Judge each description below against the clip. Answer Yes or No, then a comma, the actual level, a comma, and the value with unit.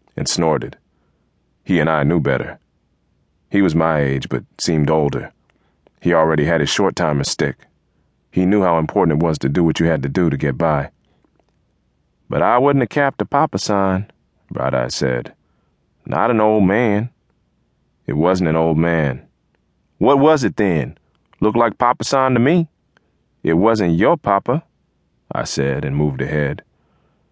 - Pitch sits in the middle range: No, very low, 95 Hz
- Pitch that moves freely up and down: Yes, wide, 7.2 semitones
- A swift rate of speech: No, average, 165 wpm